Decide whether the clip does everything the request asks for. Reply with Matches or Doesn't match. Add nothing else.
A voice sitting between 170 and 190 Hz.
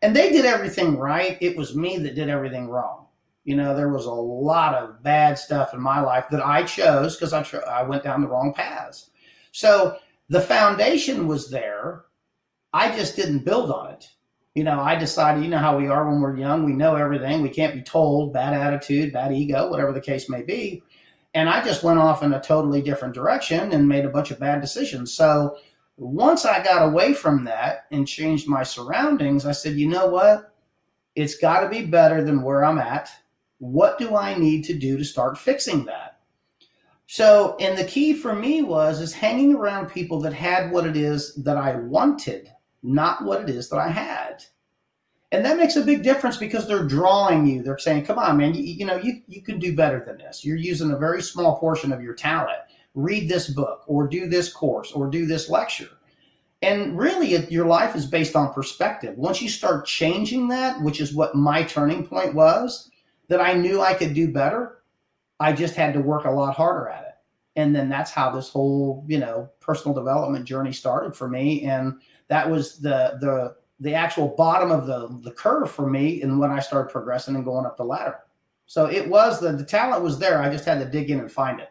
Doesn't match